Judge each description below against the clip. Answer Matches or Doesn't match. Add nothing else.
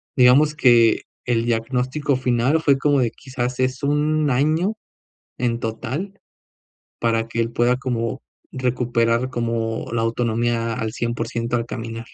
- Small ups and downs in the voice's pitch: Matches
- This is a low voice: Matches